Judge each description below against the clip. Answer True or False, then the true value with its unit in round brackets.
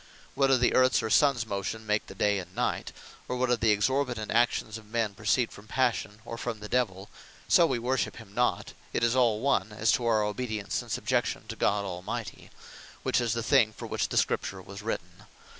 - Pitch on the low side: True (110 Hz)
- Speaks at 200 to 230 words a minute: True (205 wpm)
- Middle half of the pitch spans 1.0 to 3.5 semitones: True (2.8 semitones)